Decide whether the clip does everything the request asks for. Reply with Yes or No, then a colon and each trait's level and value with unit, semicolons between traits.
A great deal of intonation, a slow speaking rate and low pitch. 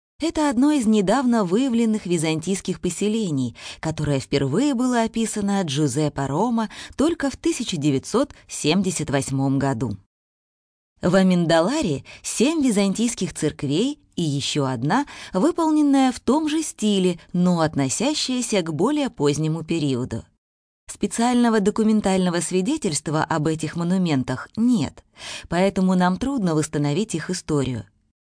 No: wide, 8.0 semitones; slow, 105 wpm; medium, 185 Hz